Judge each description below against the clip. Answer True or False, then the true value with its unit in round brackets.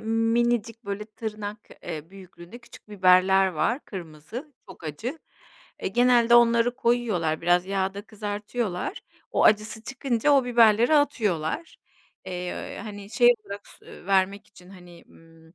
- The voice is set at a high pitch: True (210 Hz)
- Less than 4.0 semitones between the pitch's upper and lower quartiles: False (4.4 semitones)